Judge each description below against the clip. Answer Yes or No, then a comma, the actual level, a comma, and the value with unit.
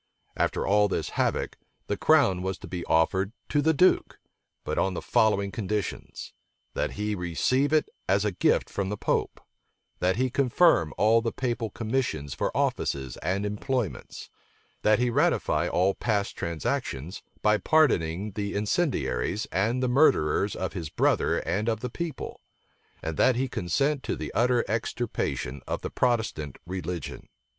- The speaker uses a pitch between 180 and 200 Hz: No, low, 105 Hz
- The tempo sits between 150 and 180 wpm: Yes, average, 155 wpm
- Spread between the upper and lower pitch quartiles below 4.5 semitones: No, average, 5.3 semitones